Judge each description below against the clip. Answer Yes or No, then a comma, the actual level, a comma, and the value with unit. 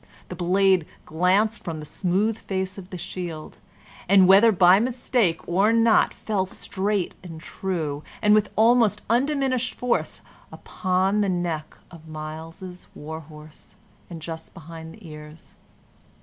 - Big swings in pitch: No, average, 4.5 semitones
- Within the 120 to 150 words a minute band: Yes, slow, 135 wpm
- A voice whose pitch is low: No, medium, 185 Hz